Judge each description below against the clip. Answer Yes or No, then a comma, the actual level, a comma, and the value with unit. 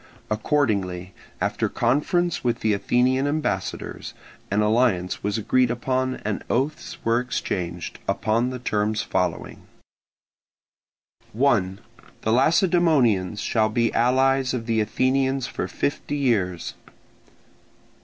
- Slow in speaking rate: Yes, slow, 105 wpm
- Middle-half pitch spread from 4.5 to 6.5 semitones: No, average, 4.1 semitones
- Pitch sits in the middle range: No, low, 120 Hz